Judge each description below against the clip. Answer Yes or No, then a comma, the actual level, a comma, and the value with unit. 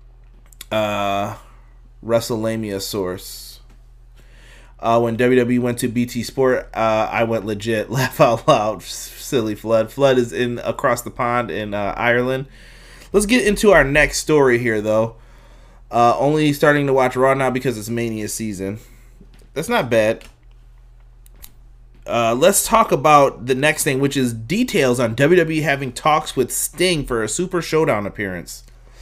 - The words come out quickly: No, average, 150 wpm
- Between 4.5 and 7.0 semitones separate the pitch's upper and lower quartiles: No, average, 3.1 semitones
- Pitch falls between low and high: No, low, 120 Hz